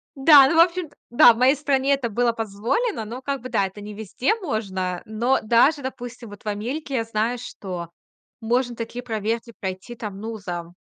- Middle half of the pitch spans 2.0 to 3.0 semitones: No, average, 4.1 semitones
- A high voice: Yes, high, 235 Hz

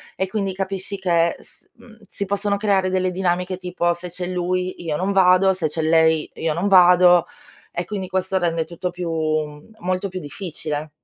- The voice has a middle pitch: Yes, medium, 180 Hz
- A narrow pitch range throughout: Yes, narrow, 2.2 semitones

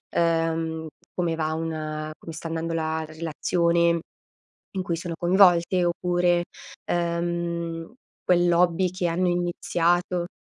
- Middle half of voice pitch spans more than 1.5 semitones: No, narrow, 1.2 semitones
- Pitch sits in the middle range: Yes, medium, 170 Hz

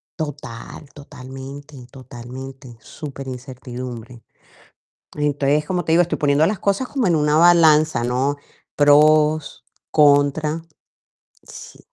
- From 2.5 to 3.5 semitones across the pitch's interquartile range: Yes, average, 2.9 semitones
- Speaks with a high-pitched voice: No, medium, 145 Hz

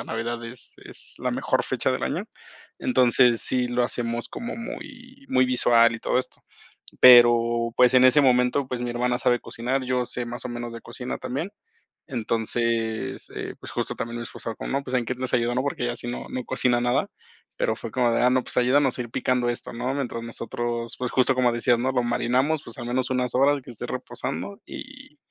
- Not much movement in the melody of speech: Yes, narrow, 1.5 semitones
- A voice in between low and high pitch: No, low, 125 Hz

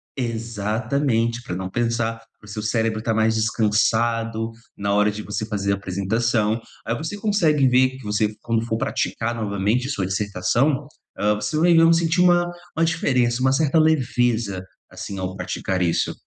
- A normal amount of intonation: Yes, average, 3.9 semitones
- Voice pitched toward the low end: Yes, low, 115 Hz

